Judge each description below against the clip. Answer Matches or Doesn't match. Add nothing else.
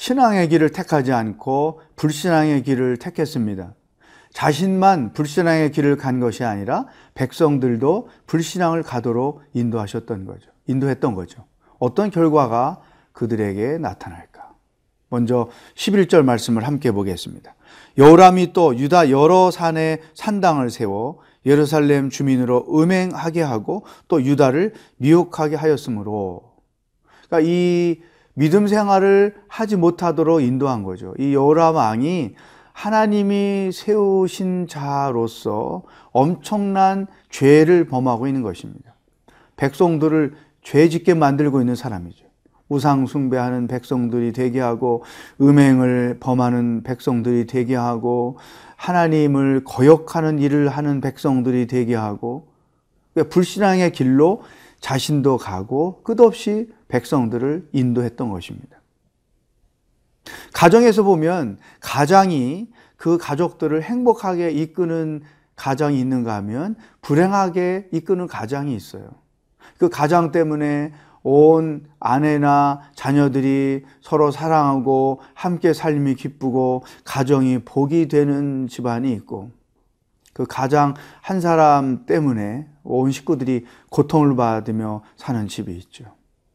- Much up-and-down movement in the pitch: Doesn't match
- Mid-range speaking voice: Matches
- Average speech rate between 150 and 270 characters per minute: Matches